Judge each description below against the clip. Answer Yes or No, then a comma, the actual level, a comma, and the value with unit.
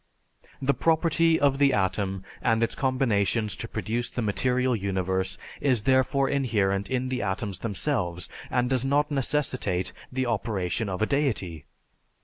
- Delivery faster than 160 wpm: No, average, 140 wpm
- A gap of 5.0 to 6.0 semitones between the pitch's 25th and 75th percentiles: Yes, wide, 5.4 semitones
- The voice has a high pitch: No, low, 120 Hz